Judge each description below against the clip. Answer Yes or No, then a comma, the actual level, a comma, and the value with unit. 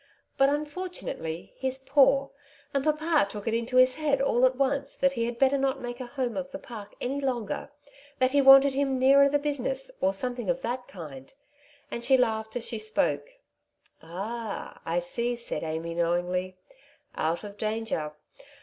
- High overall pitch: Yes, very high, 250 Hz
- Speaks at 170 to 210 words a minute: Yes, average, 175 wpm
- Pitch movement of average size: Yes, average, 4.5 semitones